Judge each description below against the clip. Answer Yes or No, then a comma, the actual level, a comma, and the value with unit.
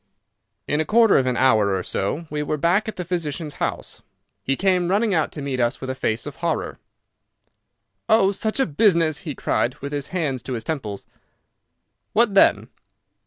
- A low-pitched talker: No, medium, 155 Hz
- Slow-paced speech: No, average, 185 wpm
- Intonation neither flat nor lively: No, wide, 5.9 semitones